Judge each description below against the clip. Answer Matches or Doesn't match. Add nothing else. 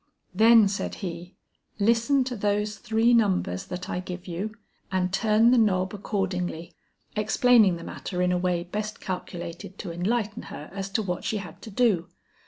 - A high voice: Matches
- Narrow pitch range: Doesn't match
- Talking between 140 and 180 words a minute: Matches